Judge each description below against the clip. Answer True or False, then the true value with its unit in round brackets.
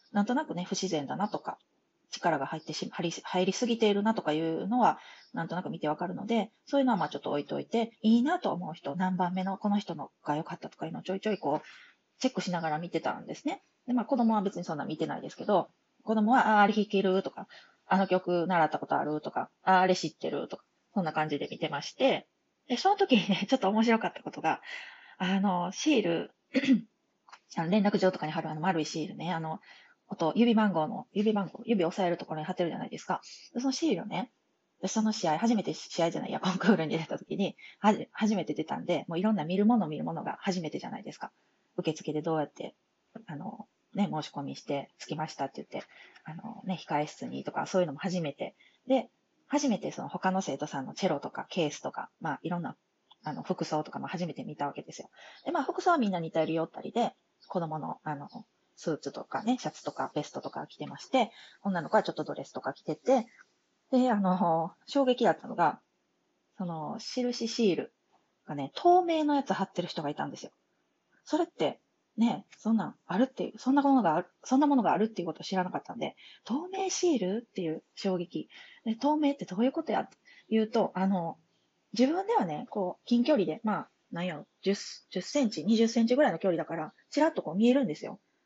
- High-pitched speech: True (195 Hz)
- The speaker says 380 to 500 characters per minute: True (415 characters per minute)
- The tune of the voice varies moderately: False (6.2 semitones)